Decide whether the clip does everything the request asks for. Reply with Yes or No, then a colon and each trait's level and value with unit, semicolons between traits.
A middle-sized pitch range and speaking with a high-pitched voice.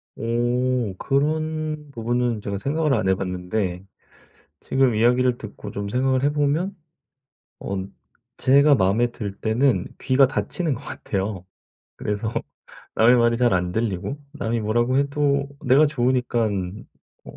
No: average, 4.9 semitones; low, 120 Hz